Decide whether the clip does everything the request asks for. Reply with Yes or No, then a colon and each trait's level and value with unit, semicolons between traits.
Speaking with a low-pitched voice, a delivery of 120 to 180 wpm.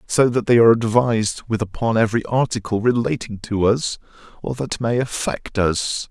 Yes: low, 115 Hz; average, 165 wpm